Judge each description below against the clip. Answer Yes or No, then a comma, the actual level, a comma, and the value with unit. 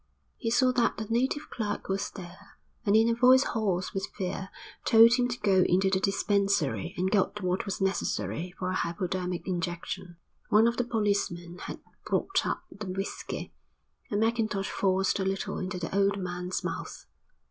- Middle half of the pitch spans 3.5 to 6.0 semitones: No, average, 3.1 semitones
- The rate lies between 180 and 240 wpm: No, average, 170 wpm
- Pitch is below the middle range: No, high, 195 Hz